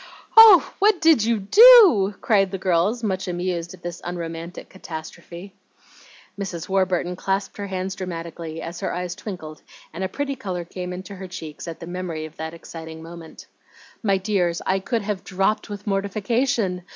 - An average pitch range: Yes, average, 3.0 semitones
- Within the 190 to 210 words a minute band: No, average, 165 wpm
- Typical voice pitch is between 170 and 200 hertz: Yes, medium, 185 Hz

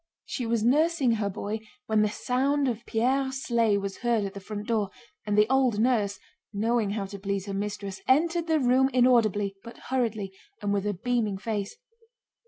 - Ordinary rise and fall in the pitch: Yes, average, 3.7 semitones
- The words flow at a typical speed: Yes, average, 175 wpm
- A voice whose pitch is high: Yes, high, 220 Hz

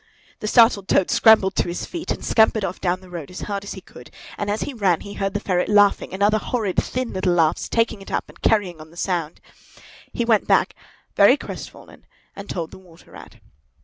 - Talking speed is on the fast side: Yes, fast, 220 wpm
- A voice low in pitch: No, high, 195 Hz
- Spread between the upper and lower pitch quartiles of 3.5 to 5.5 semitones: No, average, 3.1 semitones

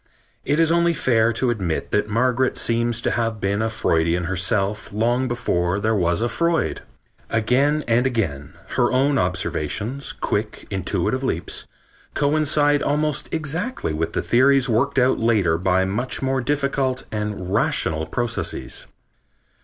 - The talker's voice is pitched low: Yes, low, 115 Hz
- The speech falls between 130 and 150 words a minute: Yes, average, 140 wpm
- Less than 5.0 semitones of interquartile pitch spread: No, wide, 5.6 semitones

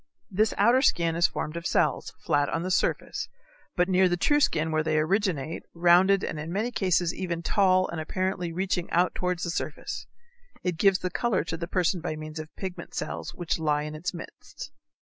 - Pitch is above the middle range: No, medium, 175 Hz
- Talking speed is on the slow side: No, average, 200 wpm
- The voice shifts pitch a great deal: No, narrow, 2.6 semitones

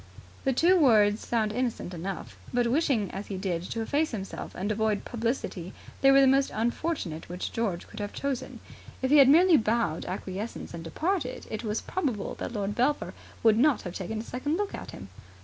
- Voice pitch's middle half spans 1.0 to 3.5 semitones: No, average, 5.2 semitones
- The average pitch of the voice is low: No, high, 230 Hz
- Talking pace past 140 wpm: Yes, average, 195 wpm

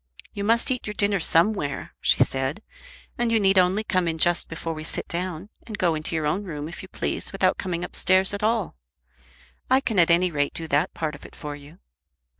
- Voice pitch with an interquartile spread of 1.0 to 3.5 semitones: No, average, 4.1 semitones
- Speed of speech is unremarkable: No, fast, 220 wpm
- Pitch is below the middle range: No, medium, 180 Hz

